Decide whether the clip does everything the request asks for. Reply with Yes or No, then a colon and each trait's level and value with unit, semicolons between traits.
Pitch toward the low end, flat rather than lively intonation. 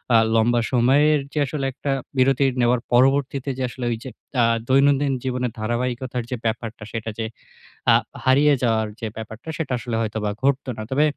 No: low, 125 Hz; average, 3.1 semitones